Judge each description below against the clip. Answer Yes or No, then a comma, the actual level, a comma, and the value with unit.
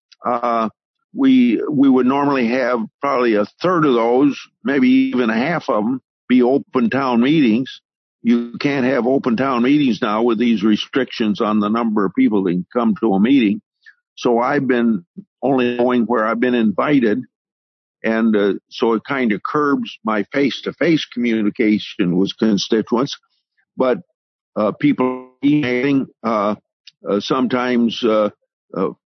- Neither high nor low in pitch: No, low, 125 Hz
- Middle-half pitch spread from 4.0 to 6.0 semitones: Yes, average, 4.4 semitones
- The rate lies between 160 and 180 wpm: No, average, 150 wpm